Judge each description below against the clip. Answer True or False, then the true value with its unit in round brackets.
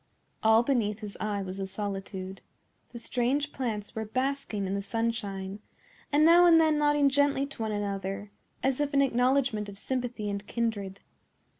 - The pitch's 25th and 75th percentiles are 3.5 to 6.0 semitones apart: True (5.2 semitones)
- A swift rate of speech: False (165 wpm)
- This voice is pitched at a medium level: False (225 Hz)